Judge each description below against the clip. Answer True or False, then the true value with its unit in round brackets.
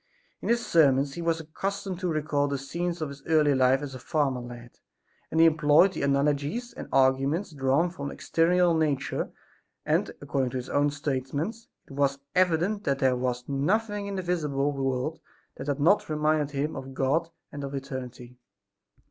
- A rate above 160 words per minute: True (175 wpm)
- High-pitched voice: False (145 Hz)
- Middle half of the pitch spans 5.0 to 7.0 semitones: False (3.6 semitones)